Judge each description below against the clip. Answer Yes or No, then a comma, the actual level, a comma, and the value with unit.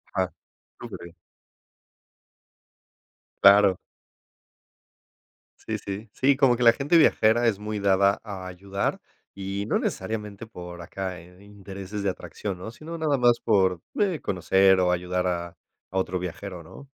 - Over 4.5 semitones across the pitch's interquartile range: No, average, 3.3 semitones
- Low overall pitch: Yes, low, 100 Hz